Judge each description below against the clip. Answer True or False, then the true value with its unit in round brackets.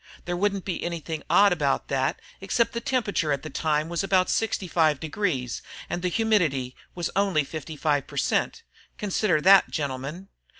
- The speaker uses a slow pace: False (160 wpm)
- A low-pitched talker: False (170 Hz)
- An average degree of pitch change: True (4.7 semitones)